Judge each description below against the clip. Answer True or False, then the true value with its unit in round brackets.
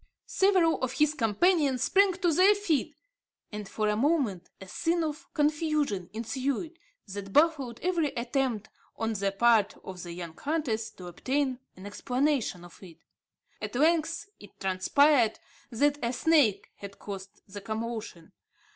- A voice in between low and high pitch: False (250 Hz)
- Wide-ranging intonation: True (7.0 semitones)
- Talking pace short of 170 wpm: True (145 wpm)